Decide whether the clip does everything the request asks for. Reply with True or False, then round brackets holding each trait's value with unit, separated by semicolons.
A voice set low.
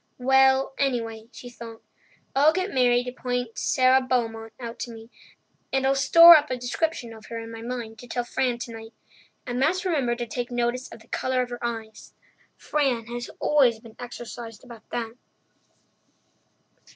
False (245 Hz)